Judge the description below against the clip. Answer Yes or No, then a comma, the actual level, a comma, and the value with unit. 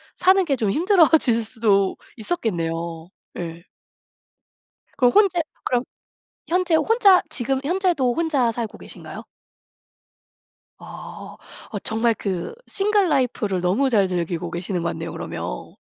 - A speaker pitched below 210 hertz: No, high, 240 Hz